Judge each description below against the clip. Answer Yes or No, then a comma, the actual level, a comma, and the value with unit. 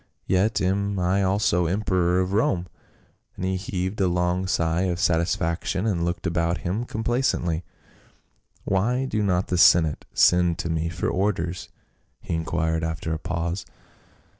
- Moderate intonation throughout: No, narrow, 2.3 semitones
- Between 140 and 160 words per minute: Yes, average, 155 wpm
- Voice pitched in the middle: No, very low, 90 Hz